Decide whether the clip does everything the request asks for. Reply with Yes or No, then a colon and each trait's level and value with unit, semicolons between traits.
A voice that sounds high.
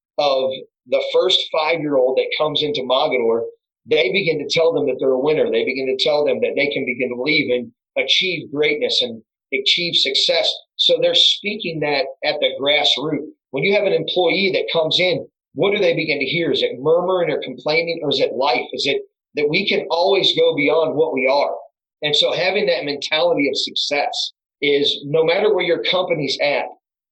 Yes: high, 200 Hz